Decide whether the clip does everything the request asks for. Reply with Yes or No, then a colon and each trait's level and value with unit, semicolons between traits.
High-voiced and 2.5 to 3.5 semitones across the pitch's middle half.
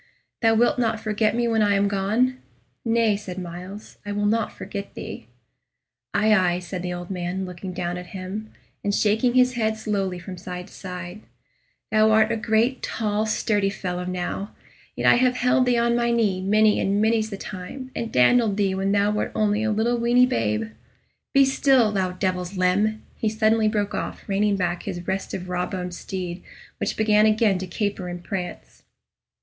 Yes: high, 205 Hz; average, 3.2 semitones